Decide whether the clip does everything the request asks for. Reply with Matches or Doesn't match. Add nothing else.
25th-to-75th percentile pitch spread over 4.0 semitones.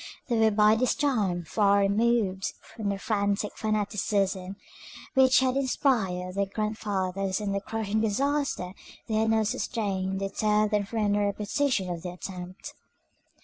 Doesn't match